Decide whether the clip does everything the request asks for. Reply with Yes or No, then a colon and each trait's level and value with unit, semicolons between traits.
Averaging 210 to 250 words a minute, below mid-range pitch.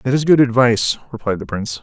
Yes: fast, 230 wpm; low, 125 Hz